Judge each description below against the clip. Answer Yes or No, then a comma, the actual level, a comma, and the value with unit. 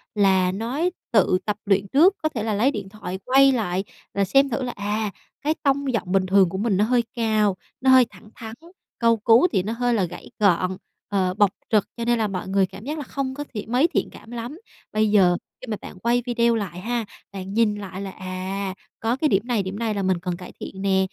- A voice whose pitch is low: No, high, 210 Hz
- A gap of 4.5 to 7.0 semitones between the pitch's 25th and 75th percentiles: No, average, 3.9 semitones